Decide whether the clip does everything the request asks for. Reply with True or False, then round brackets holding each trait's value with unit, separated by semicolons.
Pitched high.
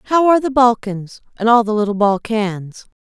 True (225 Hz)